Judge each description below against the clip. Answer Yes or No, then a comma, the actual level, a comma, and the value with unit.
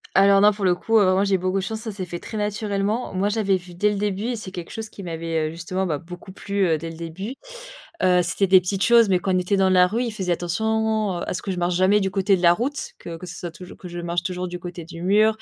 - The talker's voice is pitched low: No, high, 190 Hz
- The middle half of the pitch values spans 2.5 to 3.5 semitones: Yes, average, 2.9 semitones